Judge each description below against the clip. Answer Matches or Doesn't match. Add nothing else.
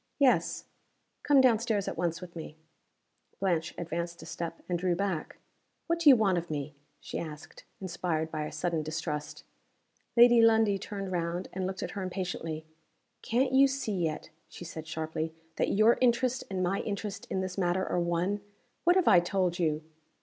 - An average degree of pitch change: Matches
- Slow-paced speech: Doesn't match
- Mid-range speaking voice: Matches